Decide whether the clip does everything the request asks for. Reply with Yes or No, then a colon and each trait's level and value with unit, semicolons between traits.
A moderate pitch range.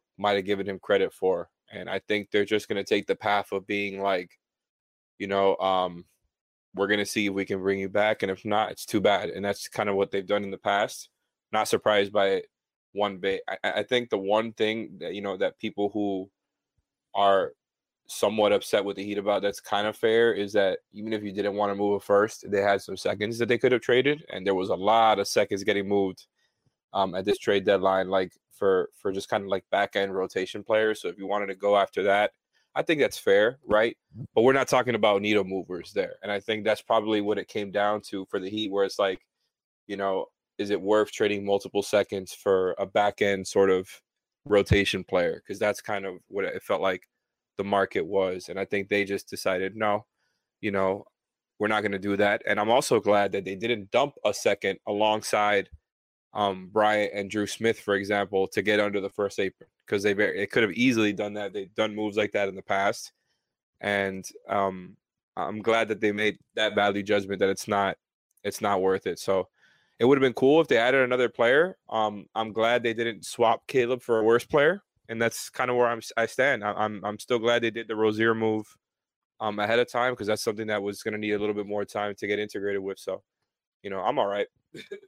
No: narrow, 1.7 semitones